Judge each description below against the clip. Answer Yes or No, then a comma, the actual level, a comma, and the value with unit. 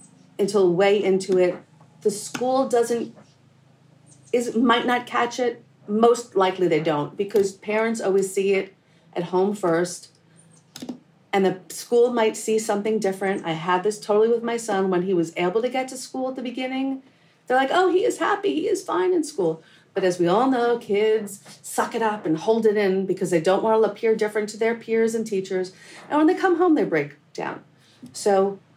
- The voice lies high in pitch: Yes, high, 210 Hz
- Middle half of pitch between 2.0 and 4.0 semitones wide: No, average, 4.6 semitones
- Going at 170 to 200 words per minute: Yes, average, 195 wpm